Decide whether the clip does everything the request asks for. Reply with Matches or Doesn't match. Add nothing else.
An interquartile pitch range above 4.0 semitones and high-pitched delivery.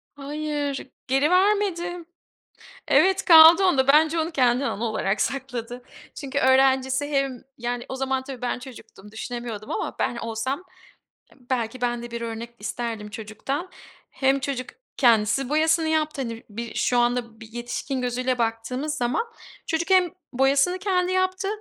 Matches